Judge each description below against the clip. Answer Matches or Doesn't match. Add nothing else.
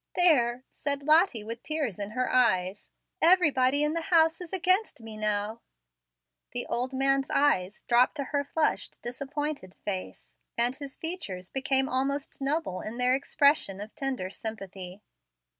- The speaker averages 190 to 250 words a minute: Doesn't match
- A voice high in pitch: Matches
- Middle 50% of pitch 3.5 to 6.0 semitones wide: Matches